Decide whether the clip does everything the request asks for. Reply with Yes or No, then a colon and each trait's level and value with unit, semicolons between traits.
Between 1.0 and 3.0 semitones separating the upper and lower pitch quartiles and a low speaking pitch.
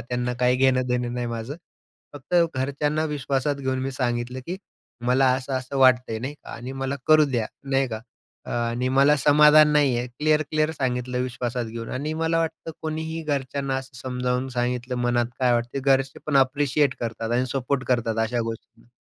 Yes: narrow, 2.5 semitones; low, 130 Hz